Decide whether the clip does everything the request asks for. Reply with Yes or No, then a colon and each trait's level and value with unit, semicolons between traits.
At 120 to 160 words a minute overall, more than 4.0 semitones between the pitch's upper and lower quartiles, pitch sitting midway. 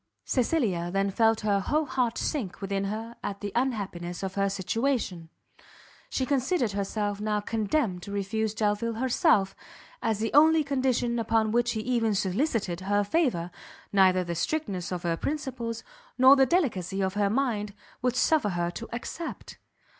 No: average, 155 wpm; average, 4.5 semitones; high, 220 Hz